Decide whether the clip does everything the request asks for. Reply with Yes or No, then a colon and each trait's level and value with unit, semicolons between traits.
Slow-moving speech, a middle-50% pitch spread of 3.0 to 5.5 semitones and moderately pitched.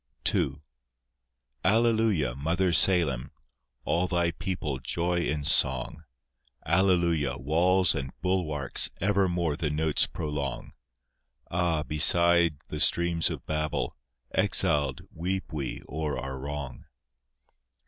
No: slow, 100 wpm; average, 3.4 semitones; very low, 80 Hz